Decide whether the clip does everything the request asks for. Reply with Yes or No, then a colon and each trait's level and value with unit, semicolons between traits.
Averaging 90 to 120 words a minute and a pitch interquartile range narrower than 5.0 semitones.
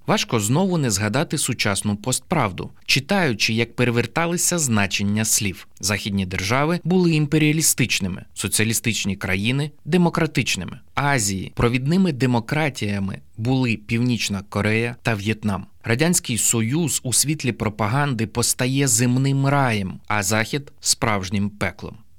No: slow, 105 wpm; wide, 5.4 semitones